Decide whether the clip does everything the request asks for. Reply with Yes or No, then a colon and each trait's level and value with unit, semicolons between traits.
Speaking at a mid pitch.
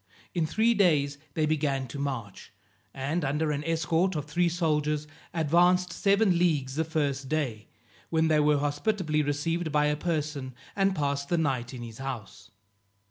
Yes: medium, 150 Hz